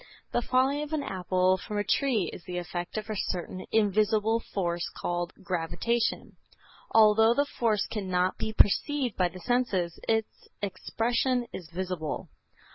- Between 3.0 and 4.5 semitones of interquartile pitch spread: Yes, average, 4.2 semitones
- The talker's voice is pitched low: No, high, 205 Hz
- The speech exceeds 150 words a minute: No, average, 145 wpm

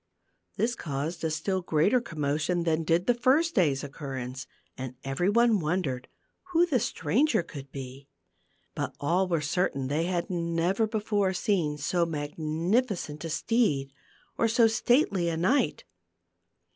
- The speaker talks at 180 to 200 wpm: No, average, 145 wpm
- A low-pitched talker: No, medium, 170 Hz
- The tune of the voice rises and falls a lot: Yes, wide, 6.1 semitones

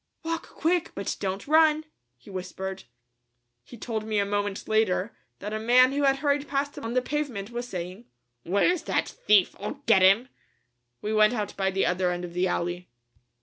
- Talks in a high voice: Yes, high, 215 Hz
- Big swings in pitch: Yes, wide, 6.0 semitones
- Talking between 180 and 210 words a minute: Yes, average, 190 wpm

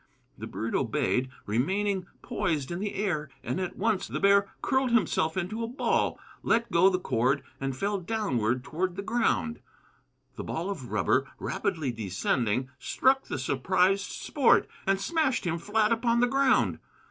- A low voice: No, medium, 185 Hz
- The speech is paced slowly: No, average, 160 wpm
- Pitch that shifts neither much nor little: No, wide, 8.3 semitones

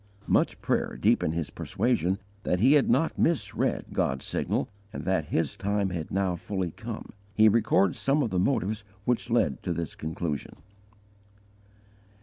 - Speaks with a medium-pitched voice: No, very low, 95 Hz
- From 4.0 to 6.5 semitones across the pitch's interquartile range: Yes, average, 5.2 semitones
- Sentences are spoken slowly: No, average, 150 wpm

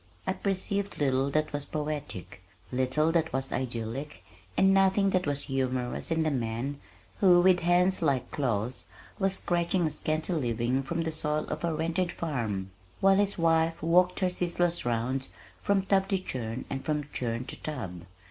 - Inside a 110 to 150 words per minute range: No, average, 165 wpm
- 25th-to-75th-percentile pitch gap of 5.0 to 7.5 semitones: Yes, wide, 5.4 semitones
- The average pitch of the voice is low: No, medium, 155 Hz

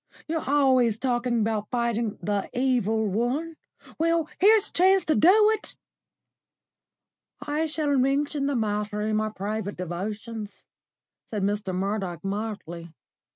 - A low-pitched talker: No, high, 230 Hz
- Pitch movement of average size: No, wide, 5.9 semitones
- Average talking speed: No, slow, 125 wpm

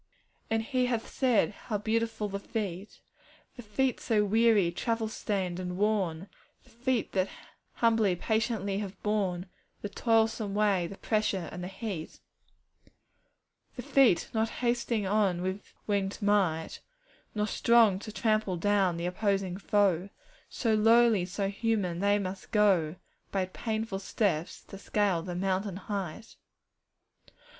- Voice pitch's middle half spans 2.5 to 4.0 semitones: Yes, average, 2.9 semitones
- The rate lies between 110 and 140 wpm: Yes, slow, 135 wpm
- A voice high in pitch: Yes, high, 205 Hz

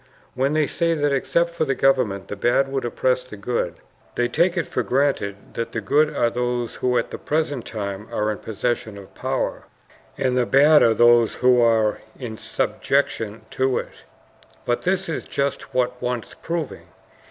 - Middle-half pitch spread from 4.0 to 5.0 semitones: No, average, 3.6 semitones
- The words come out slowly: No, average, 180 wpm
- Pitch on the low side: Yes, low, 125 Hz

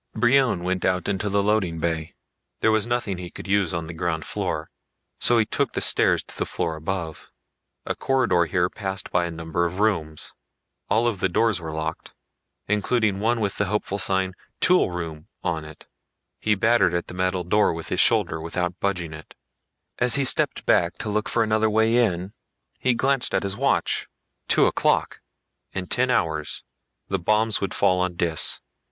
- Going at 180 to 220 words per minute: Yes, average, 185 wpm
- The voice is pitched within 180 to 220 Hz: No, very low, 95 Hz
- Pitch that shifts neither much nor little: Yes, average, 4.2 semitones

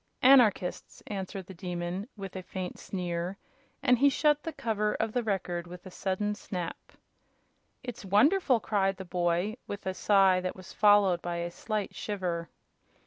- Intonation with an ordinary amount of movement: Yes, average, 3.1 semitones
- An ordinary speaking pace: Yes, average, 160 wpm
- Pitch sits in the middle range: No, high, 195 Hz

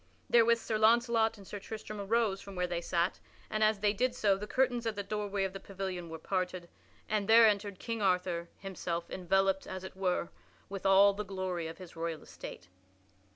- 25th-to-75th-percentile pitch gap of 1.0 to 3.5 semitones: Yes, average, 2.9 semitones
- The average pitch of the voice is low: No, high, 195 Hz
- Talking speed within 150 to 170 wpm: No, average, 200 wpm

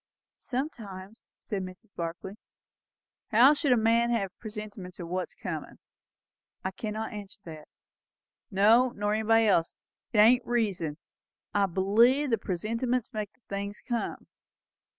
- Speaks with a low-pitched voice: No, high, 210 Hz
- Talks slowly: Yes, slow, 130 wpm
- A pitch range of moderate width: Yes, average, 3.4 semitones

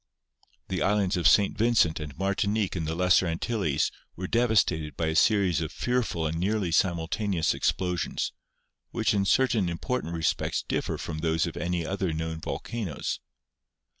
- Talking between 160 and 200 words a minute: No, average, 150 wpm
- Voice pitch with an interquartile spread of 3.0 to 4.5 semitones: Yes, average, 4.1 semitones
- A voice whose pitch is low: Yes, very low, 90 Hz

